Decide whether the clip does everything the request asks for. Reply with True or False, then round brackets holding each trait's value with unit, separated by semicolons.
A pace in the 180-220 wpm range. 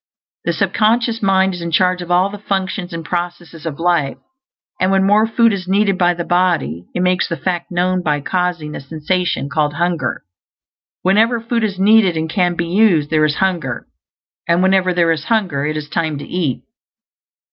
True (190 wpm)